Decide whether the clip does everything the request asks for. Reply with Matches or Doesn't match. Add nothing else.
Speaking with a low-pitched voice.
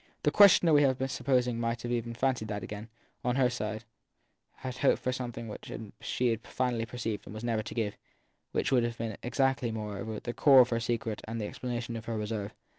Matches